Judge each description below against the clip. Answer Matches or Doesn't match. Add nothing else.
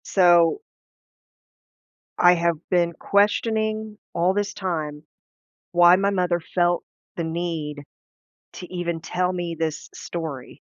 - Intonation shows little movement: Matches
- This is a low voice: Doesn't match